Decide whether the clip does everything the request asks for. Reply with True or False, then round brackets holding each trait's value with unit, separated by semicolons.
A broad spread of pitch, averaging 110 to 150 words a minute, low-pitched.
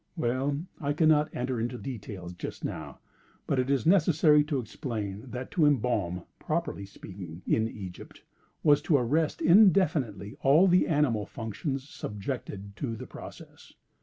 True (6.0 semitones; 140 wpm; 130 Hz)